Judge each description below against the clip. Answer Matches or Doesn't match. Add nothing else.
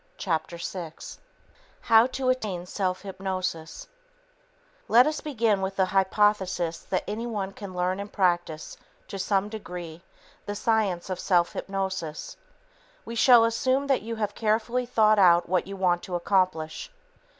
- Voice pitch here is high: Matches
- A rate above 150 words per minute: Doesn't match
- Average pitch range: Matches